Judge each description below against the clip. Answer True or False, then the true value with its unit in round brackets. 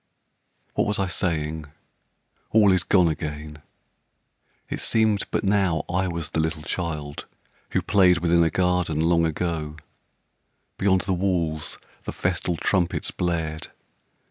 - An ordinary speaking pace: False (130 wpm)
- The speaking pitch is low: True (85 Hz)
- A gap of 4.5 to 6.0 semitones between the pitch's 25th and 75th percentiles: False (2.8 semitones)